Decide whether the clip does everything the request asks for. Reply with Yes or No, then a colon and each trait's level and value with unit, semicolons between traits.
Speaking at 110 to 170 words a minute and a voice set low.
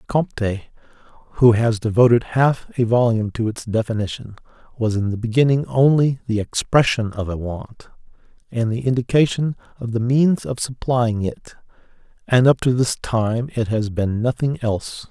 Yes: average, 155 wpm; low, 120 Hz